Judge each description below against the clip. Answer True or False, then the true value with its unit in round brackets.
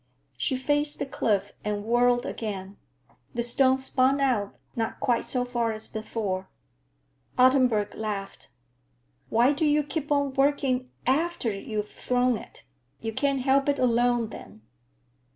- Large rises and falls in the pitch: False (3.9 semitones)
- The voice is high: True (245 Hz)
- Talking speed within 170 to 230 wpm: False (135 wpm)